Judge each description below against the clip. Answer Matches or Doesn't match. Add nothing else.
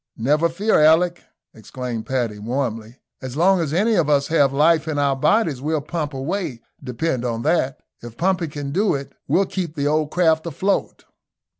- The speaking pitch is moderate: Matches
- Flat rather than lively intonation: Doesn't match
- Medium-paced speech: Matches